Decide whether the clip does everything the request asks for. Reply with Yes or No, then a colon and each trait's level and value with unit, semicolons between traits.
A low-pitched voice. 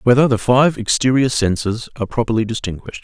Yes: low, 120 Hz